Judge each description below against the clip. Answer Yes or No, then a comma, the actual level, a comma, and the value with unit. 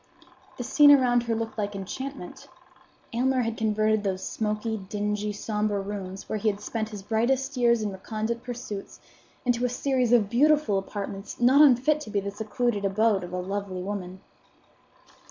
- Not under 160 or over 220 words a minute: Yes, average, 165 wpm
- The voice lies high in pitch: Yes, high, 215 Hz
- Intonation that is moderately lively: Yes, average, 3.3 semitones